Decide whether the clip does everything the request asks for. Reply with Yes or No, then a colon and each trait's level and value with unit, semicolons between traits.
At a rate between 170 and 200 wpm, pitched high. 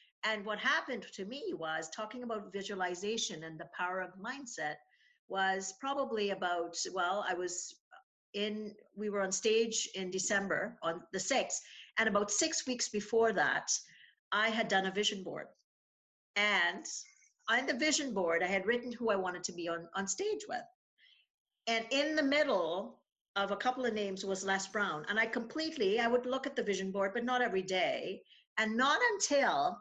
Yes: average, 175 wpm; high, 210 Hz